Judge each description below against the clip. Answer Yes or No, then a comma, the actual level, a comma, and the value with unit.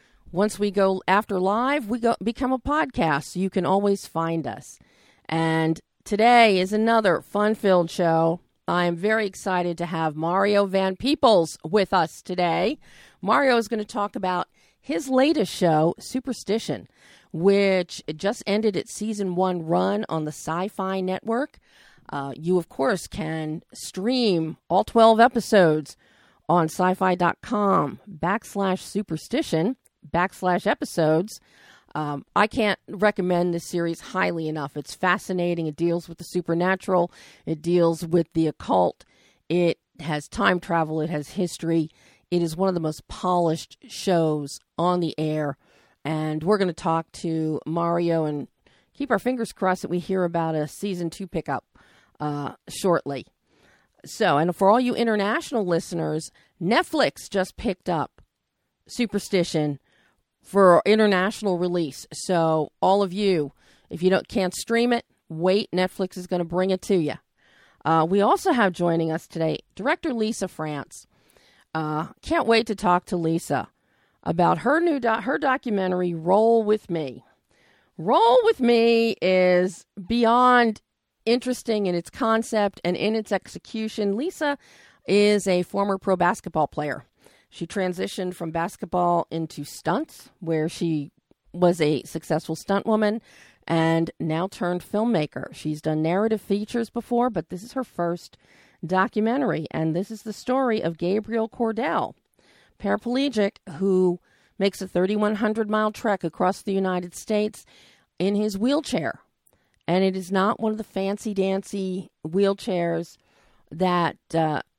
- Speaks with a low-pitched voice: No, medium, 185 Hz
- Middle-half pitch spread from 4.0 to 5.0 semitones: Yes, average, 4.4 semitones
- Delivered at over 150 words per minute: No, average, 145 wpm